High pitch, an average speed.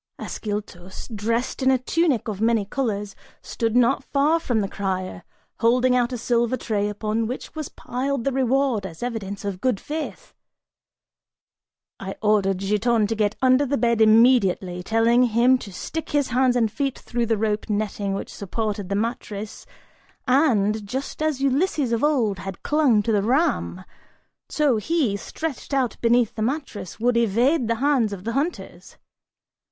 Yes: high, 230 Hz; average, 160 wpm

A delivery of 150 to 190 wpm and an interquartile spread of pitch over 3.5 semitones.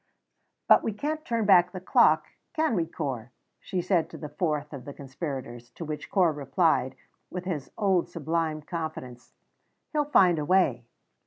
Yes: average, 165 wpm; average, 4.5 semitones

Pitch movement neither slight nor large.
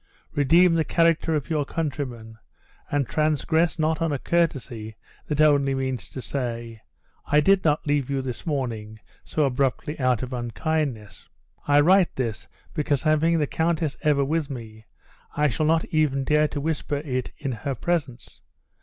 Yes: average, 3.6 semitones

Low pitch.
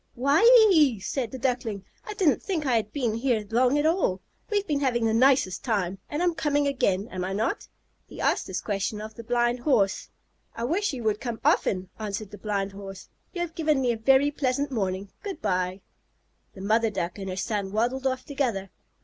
No: high, 235 Hz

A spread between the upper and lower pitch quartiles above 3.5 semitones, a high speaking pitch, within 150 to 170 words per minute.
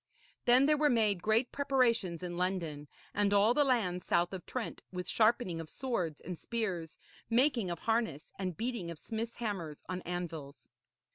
Yes: wide, 5.4 semitones; high, 200 Hz; average, 165 wpm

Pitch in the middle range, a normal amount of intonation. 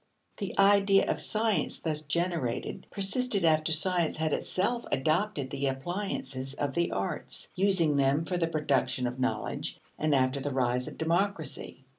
No: medium, 160 Hz; wide, 5.8 semitones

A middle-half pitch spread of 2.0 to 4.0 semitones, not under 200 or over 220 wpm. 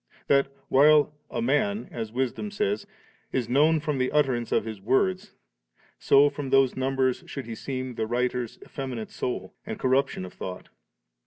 No: average, 3.0 semitones; average, 160 wpm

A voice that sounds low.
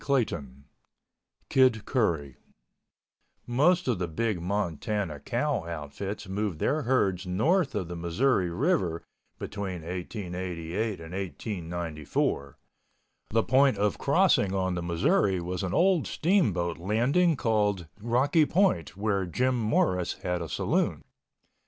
Yes: very low, 95 Hz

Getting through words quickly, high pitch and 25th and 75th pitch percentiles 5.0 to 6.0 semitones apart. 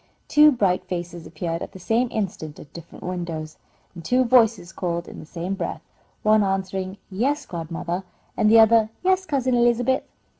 No: average, 165 wpm; high, 195 Hz; wide, 5.5 semitones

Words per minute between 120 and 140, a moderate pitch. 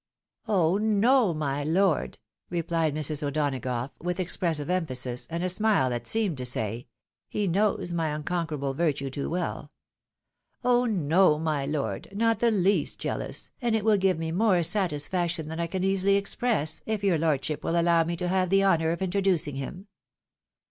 No: average, 175 wpm; medium, 170 Hz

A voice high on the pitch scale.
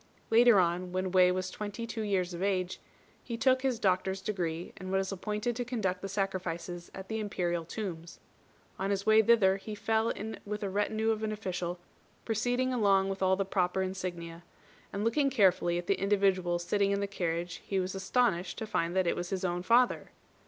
Yes: high, 195 Hz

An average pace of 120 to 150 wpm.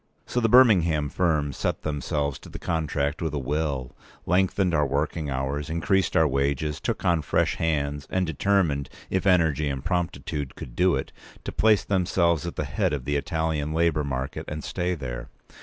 No: average, 175 wpm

